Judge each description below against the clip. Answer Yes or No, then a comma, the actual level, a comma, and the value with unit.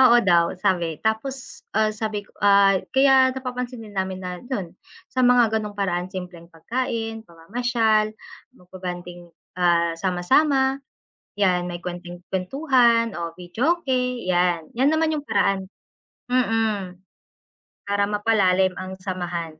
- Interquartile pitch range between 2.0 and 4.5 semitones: No, average, 5.2 semitones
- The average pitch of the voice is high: Yes, high, 200 Hz